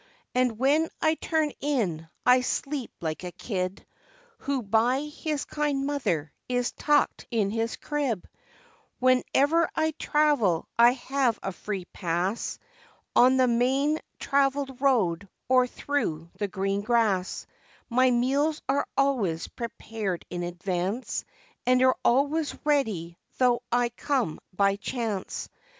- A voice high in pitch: Yes, high, 245 Hz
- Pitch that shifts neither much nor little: No, wide, 5.9 semitones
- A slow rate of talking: Yes, slow, 125 wpm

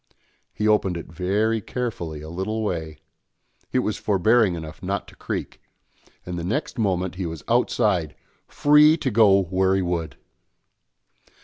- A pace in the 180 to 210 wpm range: No, average, 145 wpm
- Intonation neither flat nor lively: Yes, average, 4.1 semitones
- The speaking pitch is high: No, very low, 95 Hz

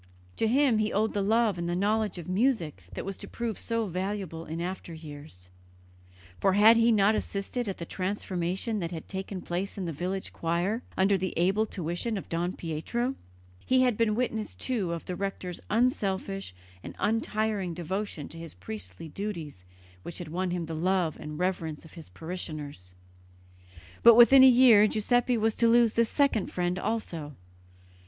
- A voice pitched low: No, high, 190 Hz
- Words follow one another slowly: No, average, 175 wpm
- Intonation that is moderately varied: Yes, average, 4.5 semitones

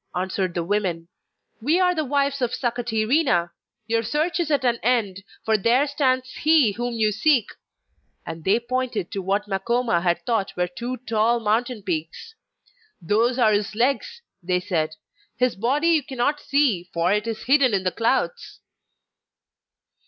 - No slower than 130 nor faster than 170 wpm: Yes, average, 160 wpm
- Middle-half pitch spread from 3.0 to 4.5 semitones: No, average, 5.2 semitones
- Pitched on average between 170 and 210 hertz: No, high, 230 Hz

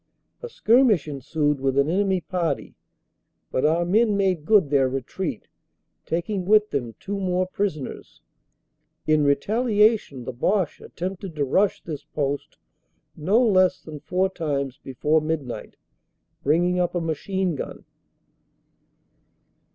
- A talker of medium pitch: Yes, medium, 170 Hz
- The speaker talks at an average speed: No, slow, 125 wpm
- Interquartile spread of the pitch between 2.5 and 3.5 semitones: No, average, 5.2 semitones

